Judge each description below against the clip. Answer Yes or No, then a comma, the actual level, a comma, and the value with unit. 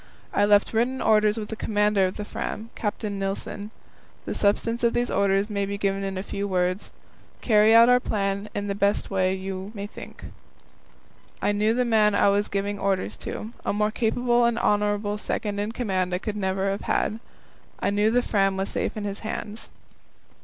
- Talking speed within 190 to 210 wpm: Yes, average, 195 wpm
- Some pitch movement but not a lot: No, narrow, 1.7 semitones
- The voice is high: Yes, high, 205 Hz